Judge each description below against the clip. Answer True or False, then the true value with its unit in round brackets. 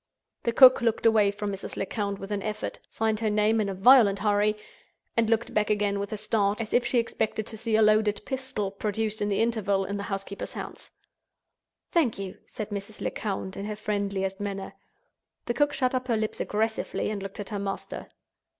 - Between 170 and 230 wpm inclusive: True (195 wpm)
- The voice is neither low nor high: False (210 Hz)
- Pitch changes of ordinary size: False (1.8 semitones)